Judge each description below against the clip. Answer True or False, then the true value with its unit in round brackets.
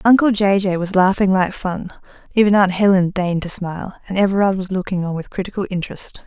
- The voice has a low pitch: False (190 Hz)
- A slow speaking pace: False (200 wpm)